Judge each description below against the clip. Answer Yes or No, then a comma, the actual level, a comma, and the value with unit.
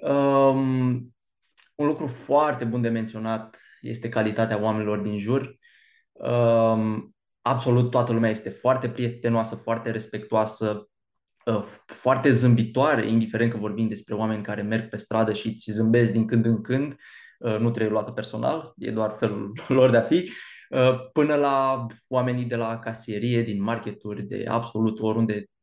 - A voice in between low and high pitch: No, low, 115 Hz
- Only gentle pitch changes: Yes, narrow, 2.3 semitones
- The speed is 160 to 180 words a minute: No, average, 150 wpm